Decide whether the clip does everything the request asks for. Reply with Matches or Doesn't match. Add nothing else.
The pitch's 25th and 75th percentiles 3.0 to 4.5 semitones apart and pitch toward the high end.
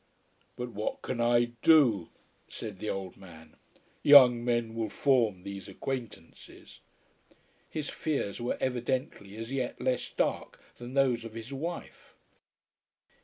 Doesn't match